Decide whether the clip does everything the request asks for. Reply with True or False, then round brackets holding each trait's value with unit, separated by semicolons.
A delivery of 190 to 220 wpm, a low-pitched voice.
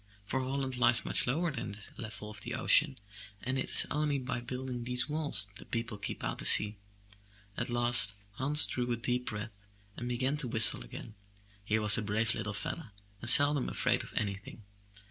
True (195 wpm; 120 Hz)